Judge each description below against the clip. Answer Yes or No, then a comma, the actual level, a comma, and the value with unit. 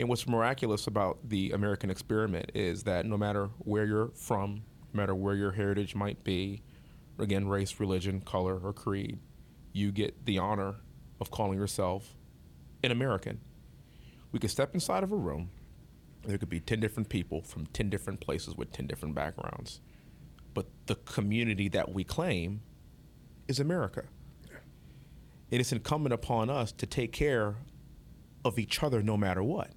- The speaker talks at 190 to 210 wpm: No, average, 160 wpm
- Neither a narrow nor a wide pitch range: Yes, average, 3.1 semitones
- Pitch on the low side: Yes, low, 105 Hz